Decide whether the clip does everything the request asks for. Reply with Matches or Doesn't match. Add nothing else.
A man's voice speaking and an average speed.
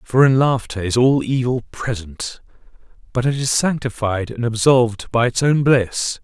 Matches